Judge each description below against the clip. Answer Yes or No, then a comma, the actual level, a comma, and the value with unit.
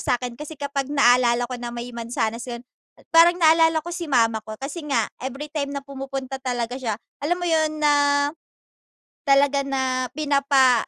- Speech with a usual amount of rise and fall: Yes, average, 3.4 semitones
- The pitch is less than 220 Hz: No, very high, 270 Hz